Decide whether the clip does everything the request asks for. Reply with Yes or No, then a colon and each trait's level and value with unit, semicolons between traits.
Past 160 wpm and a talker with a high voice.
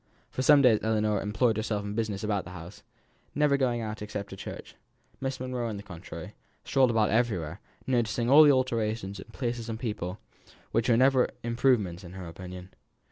No: average, 185 wpm; low, 110 Hz